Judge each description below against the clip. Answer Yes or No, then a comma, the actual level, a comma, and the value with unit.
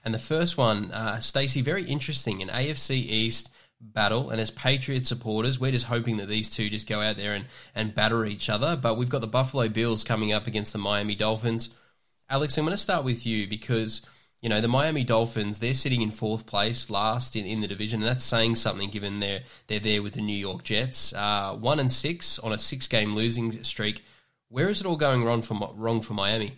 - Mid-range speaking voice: No, low, 115 Hz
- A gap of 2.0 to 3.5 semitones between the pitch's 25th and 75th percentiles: Yes, average, 3.2 semitones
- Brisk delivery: Yes, fast, 225 wpm